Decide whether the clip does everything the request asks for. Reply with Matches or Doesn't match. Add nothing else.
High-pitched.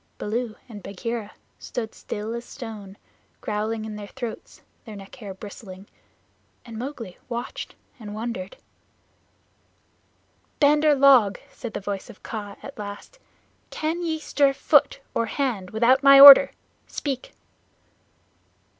Matches